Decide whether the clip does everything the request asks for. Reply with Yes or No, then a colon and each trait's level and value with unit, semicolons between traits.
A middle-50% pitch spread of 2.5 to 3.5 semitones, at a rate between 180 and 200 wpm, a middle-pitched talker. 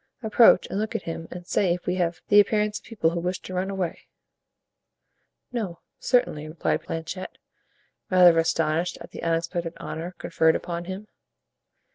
No: average, 2.8 semitones; average, 160 wpm; medium, 175 Hz